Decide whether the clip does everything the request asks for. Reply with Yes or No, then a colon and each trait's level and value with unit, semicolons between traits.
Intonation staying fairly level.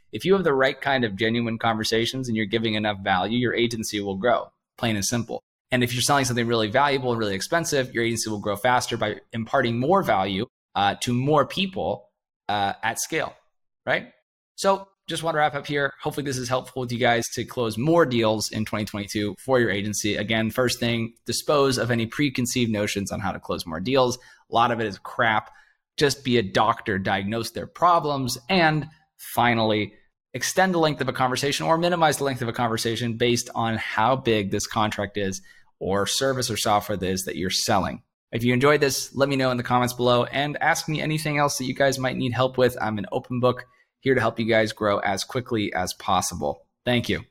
No: average, 3.9 semitones